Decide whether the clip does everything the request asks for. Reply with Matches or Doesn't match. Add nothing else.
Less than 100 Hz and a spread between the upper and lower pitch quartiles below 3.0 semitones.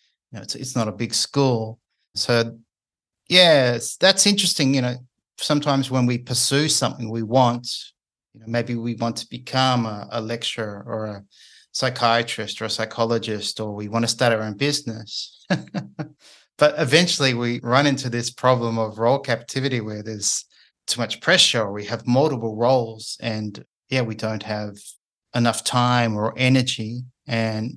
Doesn't match